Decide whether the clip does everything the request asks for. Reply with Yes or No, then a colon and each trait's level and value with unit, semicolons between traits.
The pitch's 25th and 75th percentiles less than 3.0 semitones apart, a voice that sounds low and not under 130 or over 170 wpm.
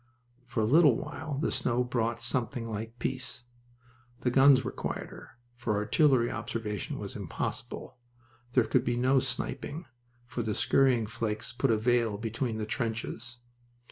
Yes: narrow, 2.4 semitones; low, 120 Hz; average, 145 wpm